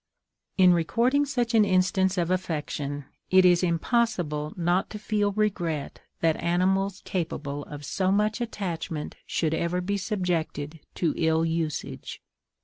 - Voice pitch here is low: No, medium, 180 Hz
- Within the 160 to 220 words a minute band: No, slow, 135 wpm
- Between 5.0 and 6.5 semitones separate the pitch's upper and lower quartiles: No, average, 3.8 semitones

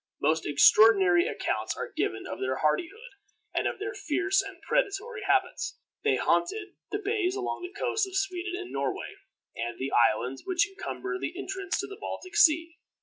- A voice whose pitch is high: Yes, very high, 375 Hz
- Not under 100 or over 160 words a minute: No, average, 170 wpm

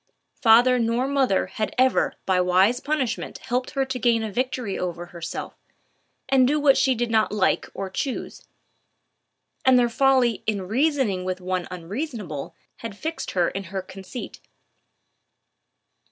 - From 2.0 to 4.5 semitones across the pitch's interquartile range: No, wide, 5.5 semitones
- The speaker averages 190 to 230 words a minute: No, average, 145 wpm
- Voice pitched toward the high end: Yes, high, 230 Hz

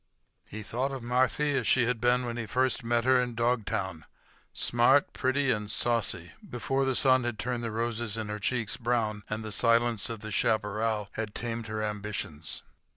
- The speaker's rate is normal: Yes, average, 175 wpm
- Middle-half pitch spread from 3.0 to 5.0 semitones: No, narrow, 2.6 semitones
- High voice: No, low, 115 Hz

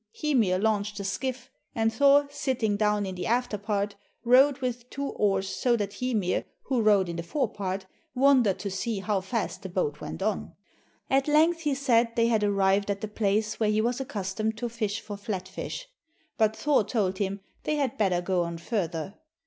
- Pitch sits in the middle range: No, high, 215 Hz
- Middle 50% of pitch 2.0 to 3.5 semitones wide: No, average, 4.1 semitones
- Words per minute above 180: Yes, average, 195 wpm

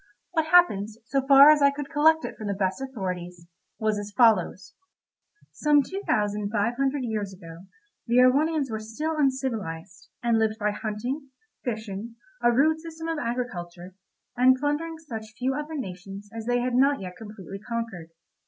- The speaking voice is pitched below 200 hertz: No, high, 235 Hz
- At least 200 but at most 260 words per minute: No, average, 165 wpm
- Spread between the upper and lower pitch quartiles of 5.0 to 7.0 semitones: Yes, wide, 5.5 semitones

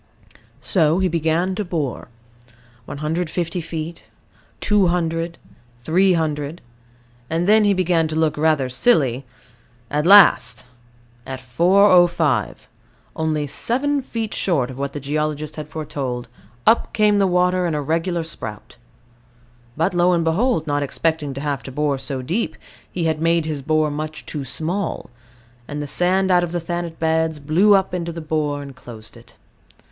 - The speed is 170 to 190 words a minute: No, average, 150 wpm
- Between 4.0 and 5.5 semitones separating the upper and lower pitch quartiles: No, average, 3.3 semitones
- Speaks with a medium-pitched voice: Yes, medium, 160 Hz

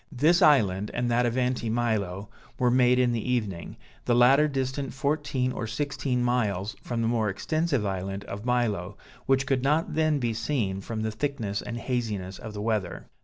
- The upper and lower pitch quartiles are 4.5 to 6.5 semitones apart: No, average, 3.9 semitones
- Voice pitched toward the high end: No, low, 120 Hz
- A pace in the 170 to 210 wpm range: Yes, average, 180 wpm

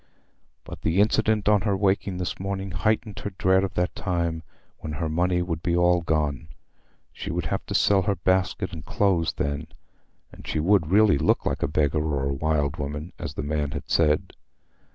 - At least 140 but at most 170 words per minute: No, average, 195 wpm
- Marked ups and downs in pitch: No, average, 4.0 semitones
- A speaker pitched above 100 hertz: No, very low, 85 Hz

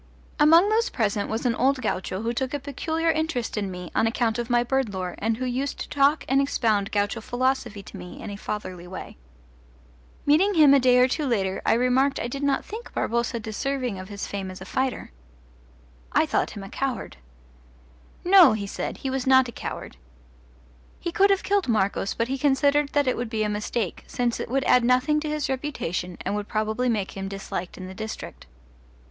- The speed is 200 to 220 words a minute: Yes, fast, 205 wpm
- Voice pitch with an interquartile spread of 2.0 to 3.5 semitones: No, average, 5.0 semitones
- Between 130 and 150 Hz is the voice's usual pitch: No, high, 245 Hz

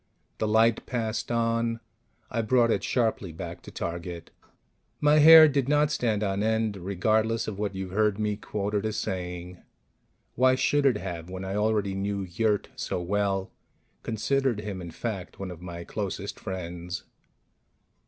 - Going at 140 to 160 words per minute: Yes, average, 155 wpm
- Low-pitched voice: Yes, low, 105 Hz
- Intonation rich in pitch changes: No, average, 3.7 semitones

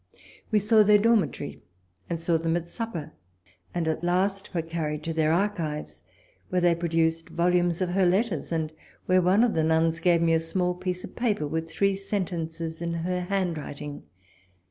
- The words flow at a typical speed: Yes, average, 180 wpm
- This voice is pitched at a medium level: Yes, medium, 170 Hz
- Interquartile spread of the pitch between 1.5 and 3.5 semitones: Yes, narrow, 2.5 semitones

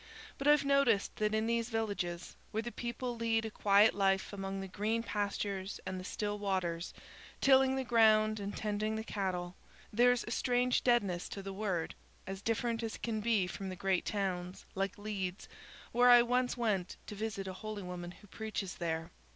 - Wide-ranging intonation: No, average, 3.2 semitones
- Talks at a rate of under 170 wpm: No, average, 185 wpm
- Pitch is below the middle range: No, high, 210 Hz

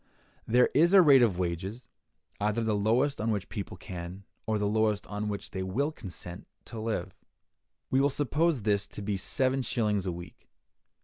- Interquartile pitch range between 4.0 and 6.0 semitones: Yes, average, 4.4 semitones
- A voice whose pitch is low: Yes, low, 105 Hz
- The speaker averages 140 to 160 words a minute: No, average, 185 wpm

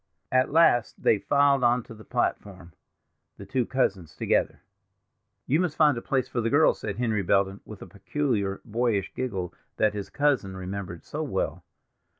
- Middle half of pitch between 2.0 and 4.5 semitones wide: No, average, 5.0 semitones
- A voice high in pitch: No, low, 110 Hz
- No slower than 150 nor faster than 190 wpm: Yes, average, 160 wpm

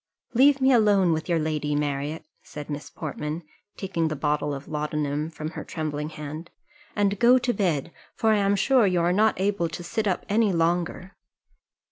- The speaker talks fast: No, average, 180 wpm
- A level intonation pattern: No, average, 5.0 semitones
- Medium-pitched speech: Yes, medium, 170 Hz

